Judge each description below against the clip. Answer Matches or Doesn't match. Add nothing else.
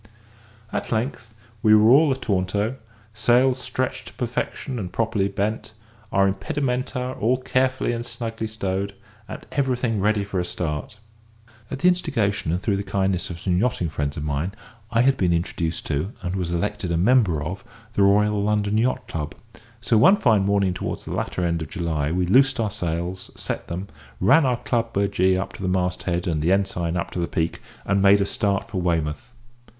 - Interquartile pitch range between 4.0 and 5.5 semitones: Matches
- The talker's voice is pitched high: Doesn't match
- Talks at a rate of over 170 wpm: Matches